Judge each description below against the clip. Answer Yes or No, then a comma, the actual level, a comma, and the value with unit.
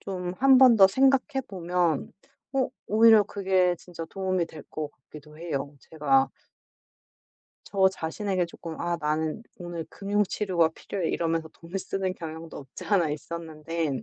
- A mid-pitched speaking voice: Yes, medium, 175 Hz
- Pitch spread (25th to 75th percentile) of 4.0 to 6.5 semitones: No, average, 3.5 semitones